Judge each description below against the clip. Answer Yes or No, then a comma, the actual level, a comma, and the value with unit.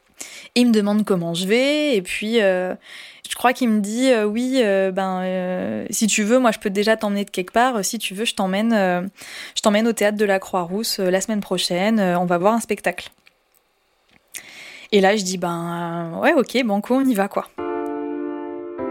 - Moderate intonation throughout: Yes, average, 3.5 semitones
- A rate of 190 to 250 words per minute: Yes, average, 215 wpm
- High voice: Yes, high, 205 Hz